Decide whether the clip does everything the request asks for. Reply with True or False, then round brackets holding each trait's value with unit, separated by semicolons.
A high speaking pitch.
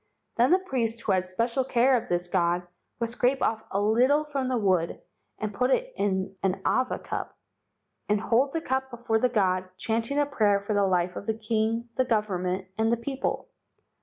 True (225 Hz)